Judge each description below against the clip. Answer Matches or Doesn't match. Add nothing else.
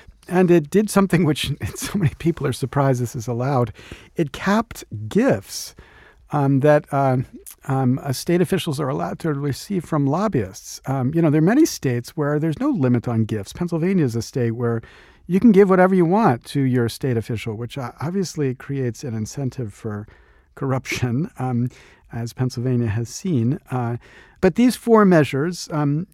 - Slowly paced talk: Doesn't match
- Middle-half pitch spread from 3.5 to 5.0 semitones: Doesn't match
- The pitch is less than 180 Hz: Matches